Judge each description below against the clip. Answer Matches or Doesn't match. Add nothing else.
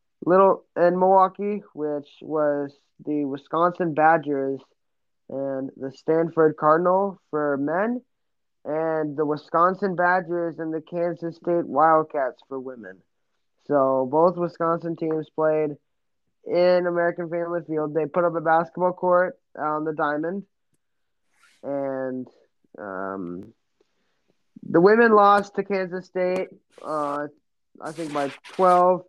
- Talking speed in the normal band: Doesn't match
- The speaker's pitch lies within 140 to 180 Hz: Matches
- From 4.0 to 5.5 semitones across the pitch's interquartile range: Doesn't match